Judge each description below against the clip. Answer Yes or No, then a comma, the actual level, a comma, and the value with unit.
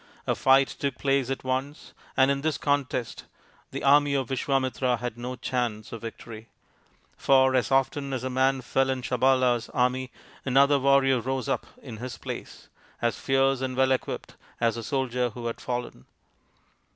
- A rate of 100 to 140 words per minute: No, average, 165 wpm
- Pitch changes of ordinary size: No, narrow, 1.7 semitones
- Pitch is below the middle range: Yes, low, 130 Hz